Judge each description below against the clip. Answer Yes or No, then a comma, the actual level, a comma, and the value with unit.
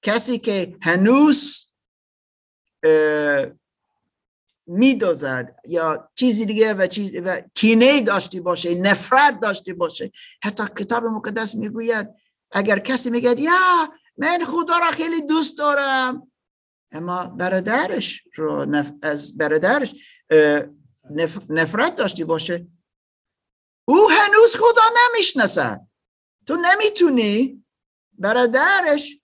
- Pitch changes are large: Yes, wide, 8.4 semitones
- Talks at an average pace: No, slow, 95 wpm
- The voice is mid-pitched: No, high, 220 Hz